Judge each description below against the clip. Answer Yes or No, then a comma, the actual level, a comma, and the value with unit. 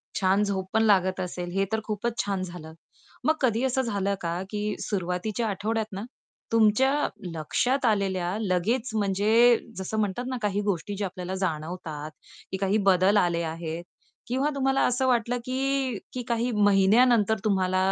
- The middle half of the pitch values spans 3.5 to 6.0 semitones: Yes, average, 3.9 semitones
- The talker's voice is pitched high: Yes, high, 205 Hz